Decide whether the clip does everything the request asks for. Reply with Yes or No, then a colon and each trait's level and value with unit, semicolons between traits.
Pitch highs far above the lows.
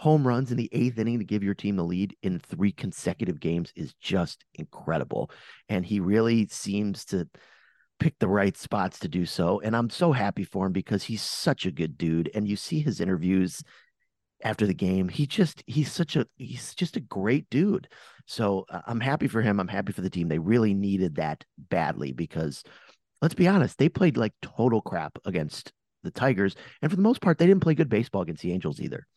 Yes: wide, 6.0 semitones